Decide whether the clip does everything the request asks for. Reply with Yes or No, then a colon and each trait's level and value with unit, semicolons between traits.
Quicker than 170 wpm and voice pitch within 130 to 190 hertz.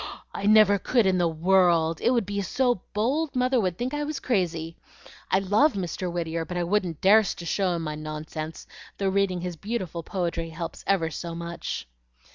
Yes: average, 195 wpm; medium, 185 Hz